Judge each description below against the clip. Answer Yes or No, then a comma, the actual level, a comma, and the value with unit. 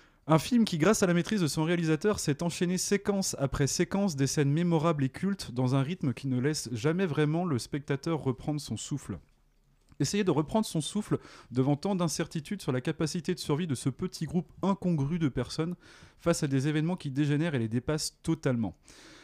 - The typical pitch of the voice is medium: Yes, medium, 155 Hz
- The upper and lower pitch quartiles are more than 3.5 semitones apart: Yes, average, 4.4 semitones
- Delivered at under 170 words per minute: No, average, 195 wpm